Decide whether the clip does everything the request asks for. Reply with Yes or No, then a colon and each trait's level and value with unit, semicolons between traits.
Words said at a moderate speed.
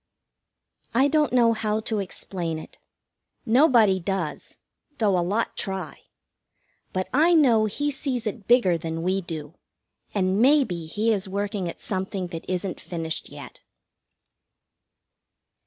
No: slow, 130 wpm